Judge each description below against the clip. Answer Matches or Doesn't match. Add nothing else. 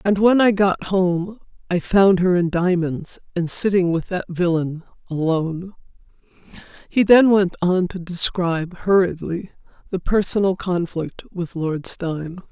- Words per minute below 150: Matches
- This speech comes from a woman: Matches